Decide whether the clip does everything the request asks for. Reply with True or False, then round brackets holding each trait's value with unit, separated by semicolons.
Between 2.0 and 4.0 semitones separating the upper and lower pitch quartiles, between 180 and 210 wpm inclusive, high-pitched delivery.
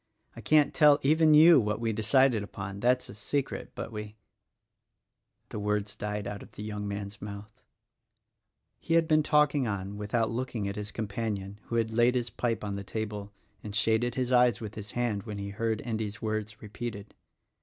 False (2.9 semitones; 195 wpm; 110 Hz)